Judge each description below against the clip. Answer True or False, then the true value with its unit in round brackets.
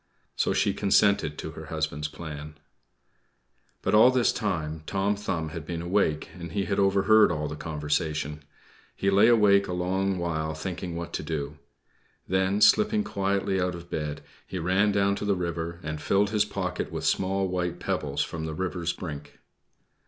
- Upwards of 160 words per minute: True (170 wpm)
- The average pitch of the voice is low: True (90 Hz)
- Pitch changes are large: False (4.0 semitones)